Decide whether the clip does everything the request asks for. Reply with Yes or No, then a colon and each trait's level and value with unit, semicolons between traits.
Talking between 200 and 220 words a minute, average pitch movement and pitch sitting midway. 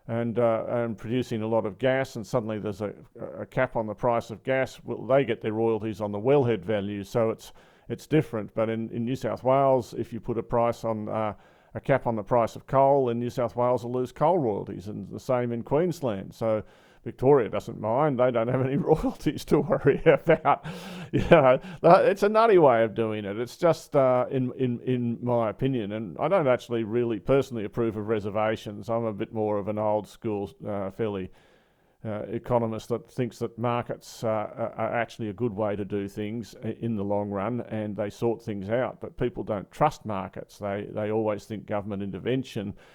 No: fast, 205 wpm; average, 3.2 semitones; low, 115 Hz